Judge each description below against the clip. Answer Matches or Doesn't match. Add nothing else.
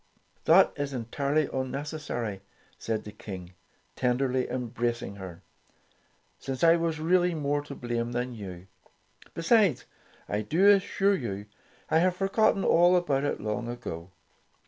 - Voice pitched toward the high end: Doesn't match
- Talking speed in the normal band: Doesn't match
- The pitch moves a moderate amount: Doesn't match